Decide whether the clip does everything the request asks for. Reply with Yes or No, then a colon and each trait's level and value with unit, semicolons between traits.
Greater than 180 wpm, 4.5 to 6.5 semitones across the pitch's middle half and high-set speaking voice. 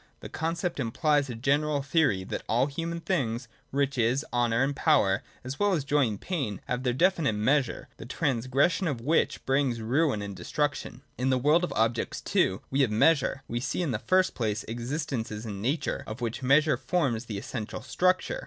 No: average, 190 wpm; average, 4.8 semitones; low, 135 Hz